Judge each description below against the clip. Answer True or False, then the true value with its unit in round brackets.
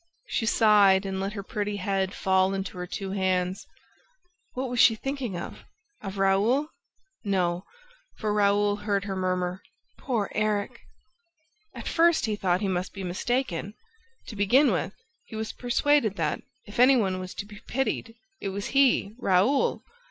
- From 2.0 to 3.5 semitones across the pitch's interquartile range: True (3.0 semitones)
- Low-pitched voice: False (205 Hz)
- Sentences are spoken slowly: False (160 wpm)